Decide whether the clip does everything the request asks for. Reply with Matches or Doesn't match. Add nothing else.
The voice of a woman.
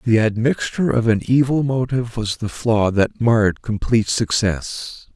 Doesn't match